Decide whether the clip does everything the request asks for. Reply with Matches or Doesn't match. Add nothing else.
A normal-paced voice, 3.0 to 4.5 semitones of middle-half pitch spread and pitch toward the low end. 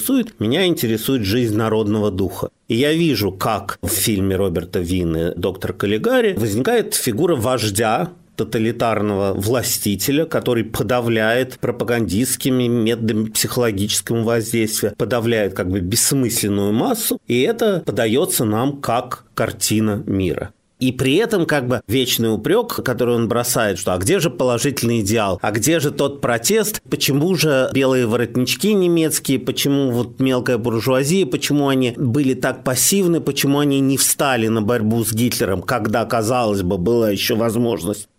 Matches